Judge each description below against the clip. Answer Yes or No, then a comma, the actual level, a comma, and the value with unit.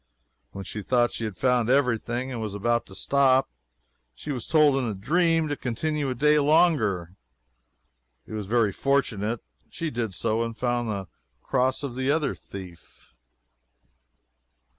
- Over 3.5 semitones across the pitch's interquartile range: Yes, average, 4.4 semitones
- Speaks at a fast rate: No, average, 160 wpm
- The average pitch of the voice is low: Yes, low, 120 Hz